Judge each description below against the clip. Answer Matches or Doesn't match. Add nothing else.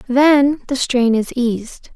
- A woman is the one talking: Matches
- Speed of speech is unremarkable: Matches